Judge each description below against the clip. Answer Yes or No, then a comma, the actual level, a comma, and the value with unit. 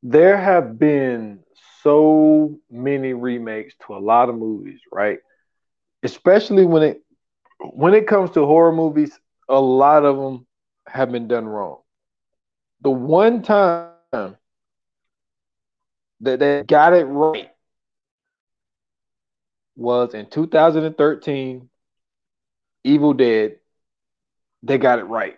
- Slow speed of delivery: Yes, slow, 110 wpm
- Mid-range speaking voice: Yes, medium, 145 Hz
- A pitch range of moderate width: Yes, average, 4.7 semitones